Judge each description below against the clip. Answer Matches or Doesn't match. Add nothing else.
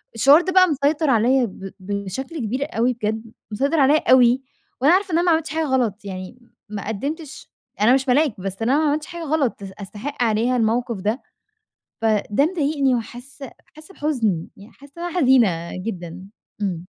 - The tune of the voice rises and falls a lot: Matches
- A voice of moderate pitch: Doesn't match